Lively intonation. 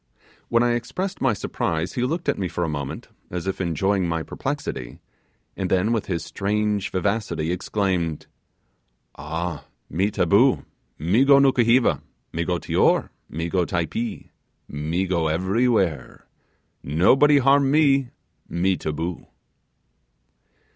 Yes: wide, 6.1 semitones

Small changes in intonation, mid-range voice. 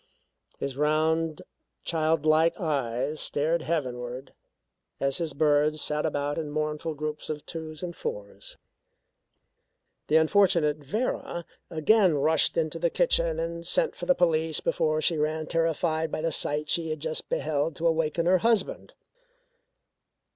Yes: narrow, 1.8 semitones; medium, 155 Hz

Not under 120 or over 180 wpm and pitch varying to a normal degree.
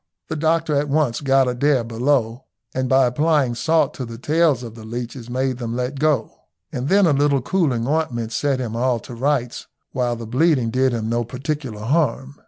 No: average, 190 wpm; average, 3.7 semitones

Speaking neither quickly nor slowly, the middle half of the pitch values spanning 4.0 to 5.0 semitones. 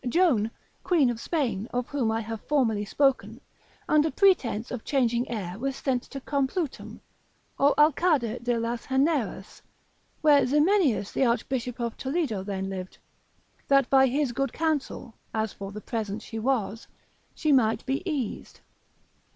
Yes: average, 145 wpm; average, 4.3 semitones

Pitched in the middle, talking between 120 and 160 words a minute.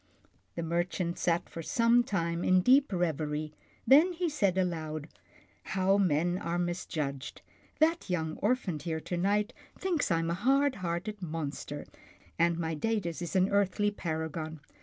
Yes: medium, 175 Hz; average, 155 wpm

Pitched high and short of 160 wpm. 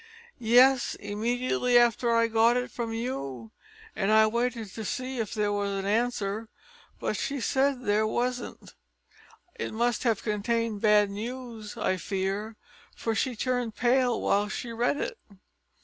Yes: high, 230 Hz; average, 150 wpm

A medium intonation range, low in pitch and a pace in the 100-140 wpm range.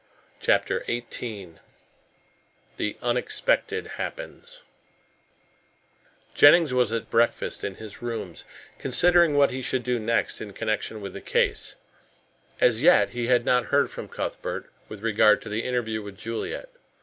Yes: average, 4.2 semitones; low, 120 Hz; slow, 135 wpm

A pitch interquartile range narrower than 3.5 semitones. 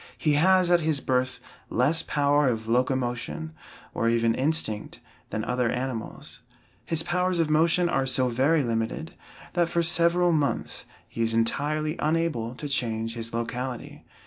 No: wide, 5.6 semitones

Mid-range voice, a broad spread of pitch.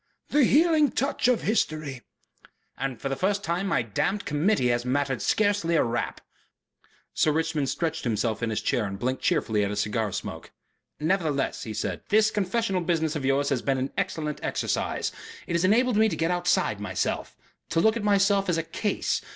Yes: medium, 160 Hz; wide, 7.6 semitones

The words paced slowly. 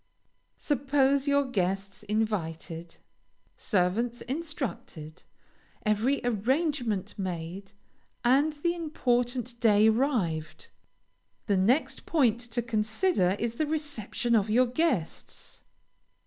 Yes: slow, 90 wpm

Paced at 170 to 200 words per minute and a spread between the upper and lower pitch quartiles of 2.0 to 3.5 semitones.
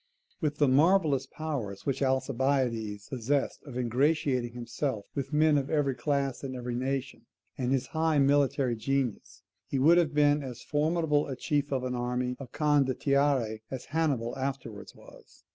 No: average, 155 wpm; average, 2.8 semitones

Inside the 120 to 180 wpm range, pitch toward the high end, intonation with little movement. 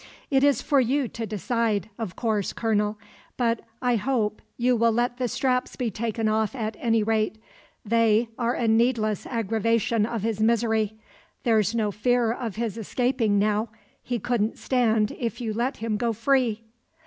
Yes: average, 165 wpm; high, 230 Hz; narrow, 2.0 semitones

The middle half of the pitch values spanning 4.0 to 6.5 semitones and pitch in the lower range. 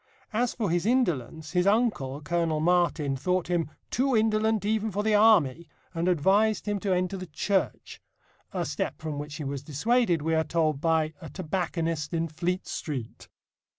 No: average, 4.9 semitones; medium, 175 Hz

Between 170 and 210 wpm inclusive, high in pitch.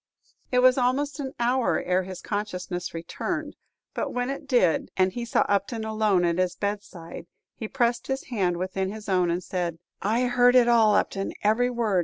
Yes: average, 185 wpm; high, 215 Hz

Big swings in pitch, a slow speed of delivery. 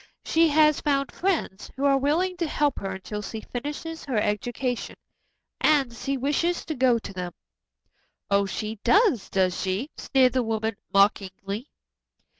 No: wide, 6.1 semitones; average, 150 wpm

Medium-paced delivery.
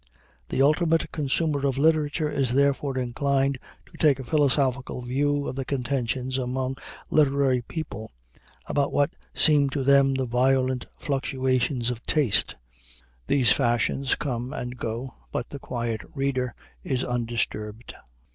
No: slow, 130 wpm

